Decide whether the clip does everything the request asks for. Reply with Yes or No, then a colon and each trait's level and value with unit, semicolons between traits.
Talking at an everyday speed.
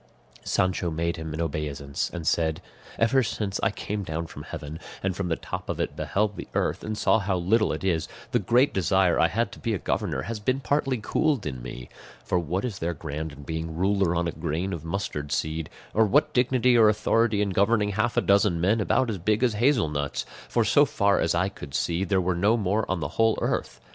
No: fast, 225 wpm